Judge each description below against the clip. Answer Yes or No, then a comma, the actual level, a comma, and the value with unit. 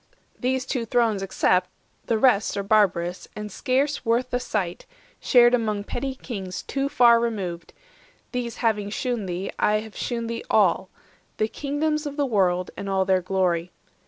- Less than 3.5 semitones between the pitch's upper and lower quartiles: No, average, 4.5 semitones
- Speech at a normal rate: Yes, average, 160 wpm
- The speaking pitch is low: No, high, 220 Hz